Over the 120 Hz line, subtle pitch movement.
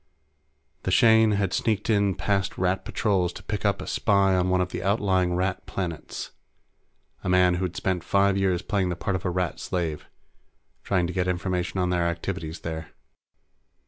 No: very low, 95 Hz; narrow, 1.8 semitones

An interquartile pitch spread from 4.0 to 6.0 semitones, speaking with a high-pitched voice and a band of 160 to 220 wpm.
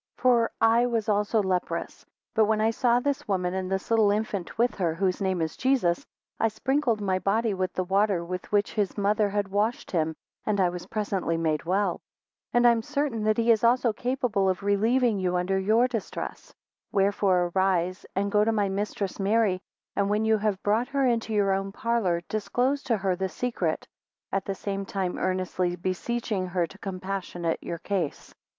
No: average, 3.3 semitones; high, 200 Hz; average, 190 wpm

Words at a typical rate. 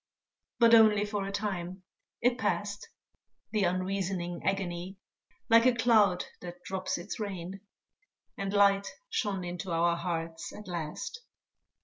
No: slow, 125 wpm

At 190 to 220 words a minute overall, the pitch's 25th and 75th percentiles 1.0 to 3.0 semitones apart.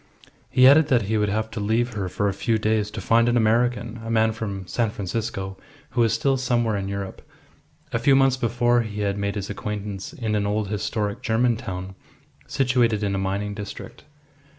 Yes: average, 200 wpm; average, 2.7 semitones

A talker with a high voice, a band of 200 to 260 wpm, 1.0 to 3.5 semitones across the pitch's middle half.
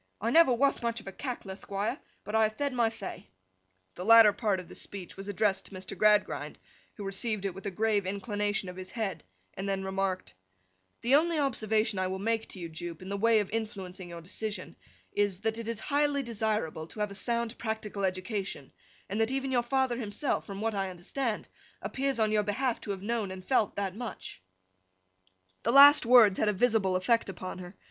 Yes: high, 210 Hz; fast, 205 wpm; average, 3.2 semitones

